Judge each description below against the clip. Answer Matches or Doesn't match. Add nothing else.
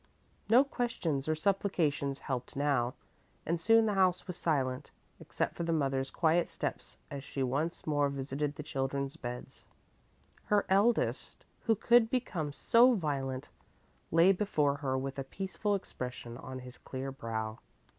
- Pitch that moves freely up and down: Matches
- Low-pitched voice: Doesn't match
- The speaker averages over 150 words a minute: Doesn't match